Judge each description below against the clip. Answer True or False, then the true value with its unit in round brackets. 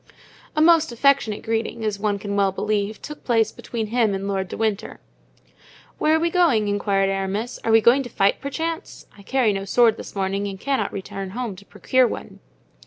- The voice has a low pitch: False (220 Hz)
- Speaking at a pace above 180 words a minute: True (195 wpm)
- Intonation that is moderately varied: True (4.1 semitones)